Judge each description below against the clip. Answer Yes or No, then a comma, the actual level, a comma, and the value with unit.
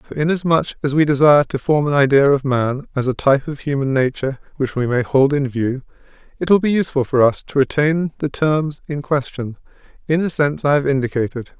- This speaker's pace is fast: Yes, fast, 210 wpm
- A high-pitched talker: No, medium, 140 Hz